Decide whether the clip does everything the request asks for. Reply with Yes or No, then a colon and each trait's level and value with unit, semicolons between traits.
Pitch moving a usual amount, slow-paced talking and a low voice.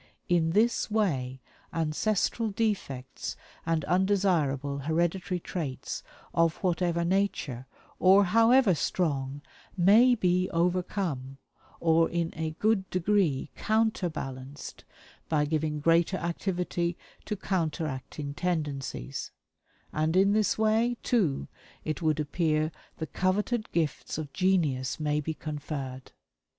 No: average, 4.3 semitones; slow, 105 wpm; medium, 170 Hz